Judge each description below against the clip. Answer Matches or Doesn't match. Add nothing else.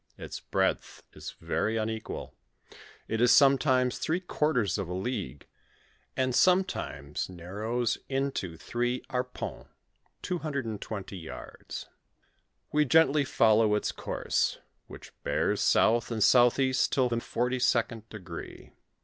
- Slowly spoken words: Matches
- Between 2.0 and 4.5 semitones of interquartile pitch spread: Matches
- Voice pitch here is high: Doesn't match